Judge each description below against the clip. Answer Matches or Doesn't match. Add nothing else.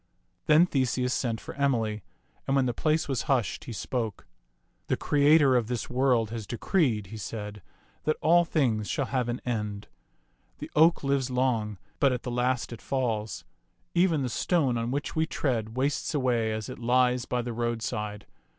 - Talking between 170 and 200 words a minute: Matches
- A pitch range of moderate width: Matches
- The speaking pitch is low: Matches